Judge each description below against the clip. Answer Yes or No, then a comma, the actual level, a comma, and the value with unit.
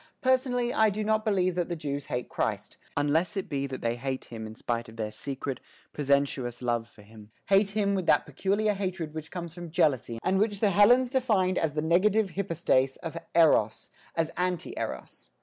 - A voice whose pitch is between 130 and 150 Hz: No, medium, 170 Hz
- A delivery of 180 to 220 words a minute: Yes, average, 195 wpm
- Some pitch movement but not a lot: No, wide, 6.8 semitones